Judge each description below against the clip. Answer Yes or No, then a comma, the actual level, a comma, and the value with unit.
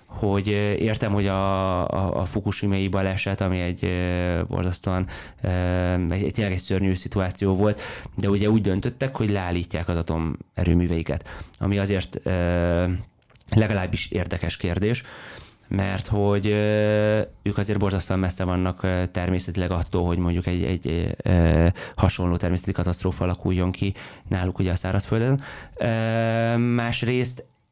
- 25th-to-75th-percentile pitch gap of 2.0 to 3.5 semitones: Yes, average, 2.8 semitones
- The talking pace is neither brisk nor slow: Yes, average, 125 wpm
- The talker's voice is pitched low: Yes, very low, 95 Hz